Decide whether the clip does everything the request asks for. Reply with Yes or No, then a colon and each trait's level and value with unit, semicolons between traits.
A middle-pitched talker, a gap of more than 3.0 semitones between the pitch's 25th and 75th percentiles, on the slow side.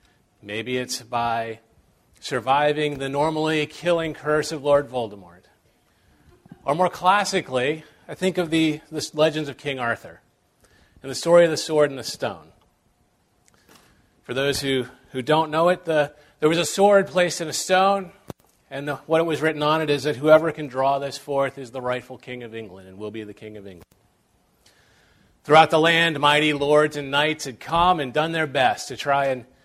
No: medium, 150 Hz; average, 3.5 semitones; average, 185 wpm